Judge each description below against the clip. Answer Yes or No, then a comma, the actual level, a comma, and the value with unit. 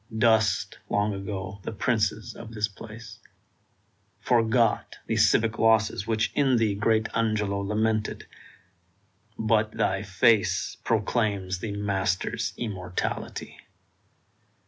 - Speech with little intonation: Yes, narrow, 2.1 semitones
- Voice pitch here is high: No, low, 110 Hz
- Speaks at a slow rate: Yes, slow, 100 wpm